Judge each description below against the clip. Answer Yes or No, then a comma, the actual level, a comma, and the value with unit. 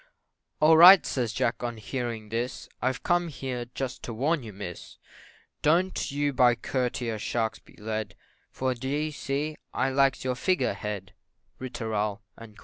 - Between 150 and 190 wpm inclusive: Yes, average, 155 wpm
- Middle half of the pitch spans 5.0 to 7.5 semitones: No, average, 4.1 semitones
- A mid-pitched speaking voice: No, low, 125 Hz